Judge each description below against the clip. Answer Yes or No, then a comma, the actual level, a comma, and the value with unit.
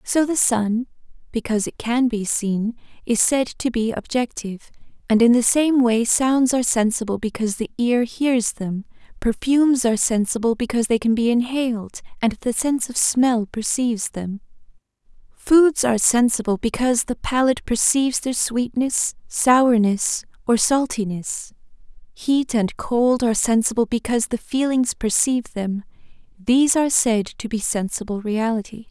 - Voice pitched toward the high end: Yes, high, 235 Hz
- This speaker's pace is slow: No, average, 145 wpm